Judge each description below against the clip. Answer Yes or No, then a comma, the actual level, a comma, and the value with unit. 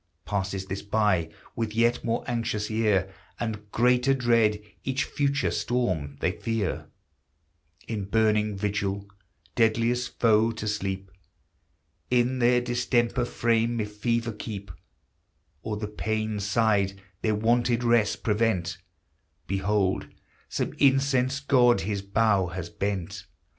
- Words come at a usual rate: No, slow, 115 wpm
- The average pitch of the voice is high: No, low, 110 Hz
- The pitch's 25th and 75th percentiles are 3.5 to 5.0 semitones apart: No, average, 2.9 semitones